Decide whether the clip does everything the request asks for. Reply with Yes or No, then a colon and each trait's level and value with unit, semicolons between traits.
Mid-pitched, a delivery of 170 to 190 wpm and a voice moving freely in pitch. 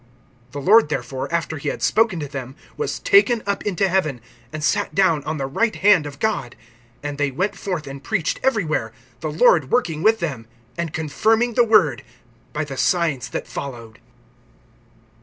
Yes: medium, 160 Hz; average, 175 wpm; wide, 6.5 semitones